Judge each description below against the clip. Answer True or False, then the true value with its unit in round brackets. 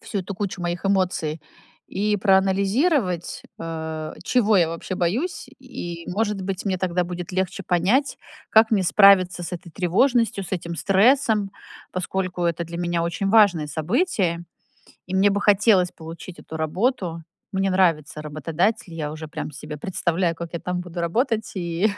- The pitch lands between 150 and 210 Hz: True (185 Hz)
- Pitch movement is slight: False (3.0 semitones)